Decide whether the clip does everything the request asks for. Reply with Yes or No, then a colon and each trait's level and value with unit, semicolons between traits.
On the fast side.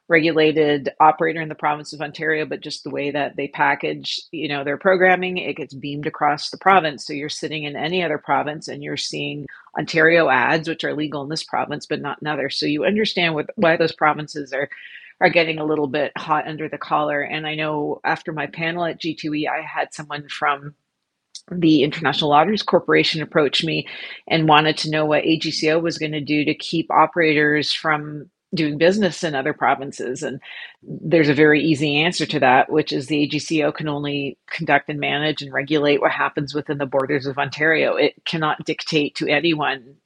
No: average, 195 wpm